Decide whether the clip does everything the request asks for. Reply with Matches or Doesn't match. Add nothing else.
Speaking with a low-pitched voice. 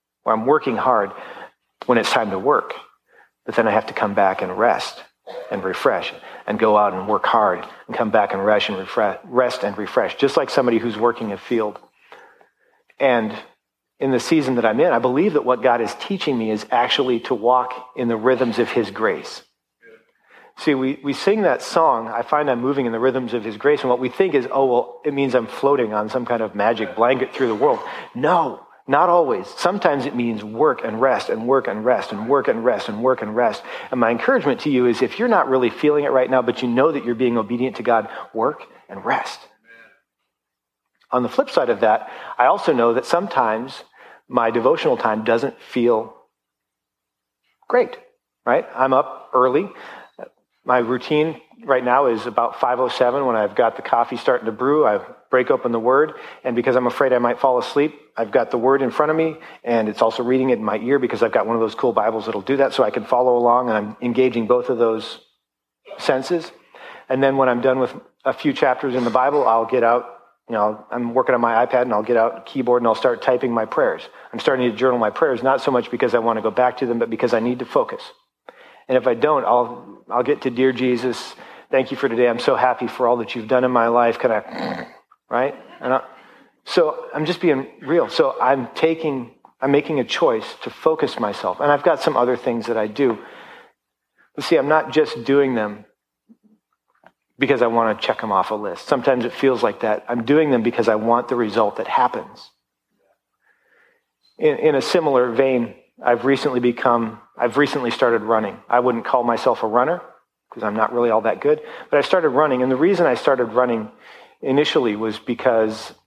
Matches